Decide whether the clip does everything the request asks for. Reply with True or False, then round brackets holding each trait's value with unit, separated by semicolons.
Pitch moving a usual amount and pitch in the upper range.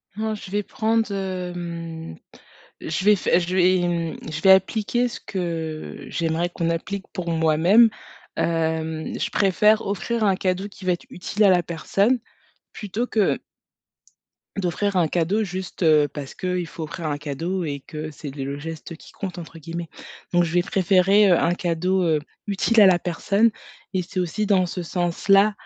False (3.2 semitones; 180 Hz)